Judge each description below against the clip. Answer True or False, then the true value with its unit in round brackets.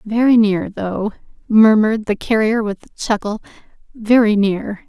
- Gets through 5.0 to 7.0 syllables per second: False (4.5 syllables/s)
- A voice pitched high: True (215 Hz)